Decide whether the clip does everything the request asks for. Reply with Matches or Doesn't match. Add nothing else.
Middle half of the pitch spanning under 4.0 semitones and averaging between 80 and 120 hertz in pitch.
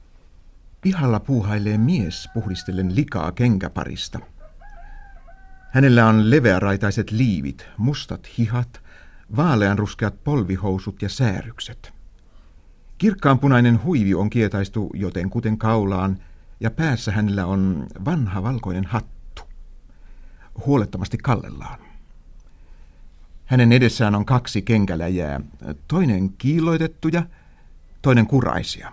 Doesn't match